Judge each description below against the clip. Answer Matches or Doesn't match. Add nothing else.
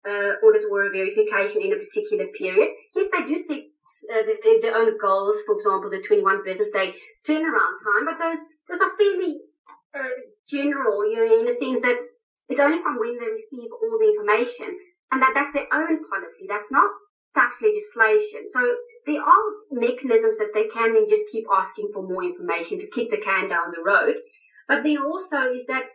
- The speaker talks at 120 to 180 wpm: Doesn't match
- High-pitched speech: Matches